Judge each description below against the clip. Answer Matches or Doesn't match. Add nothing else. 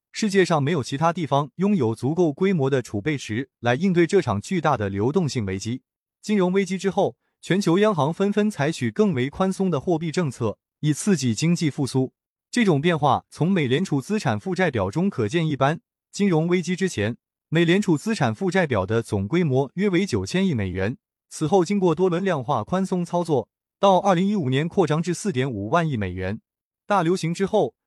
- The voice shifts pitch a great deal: Matches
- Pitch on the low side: Doesn't match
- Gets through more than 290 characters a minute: Matches